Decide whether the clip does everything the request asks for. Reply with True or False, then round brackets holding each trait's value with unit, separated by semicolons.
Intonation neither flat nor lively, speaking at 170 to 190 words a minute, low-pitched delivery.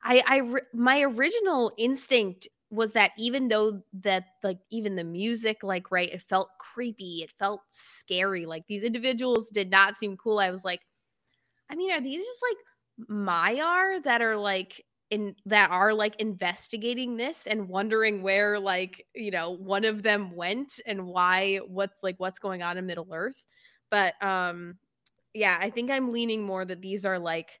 False (3.9 semitones; 175 wpm; 205 Hz)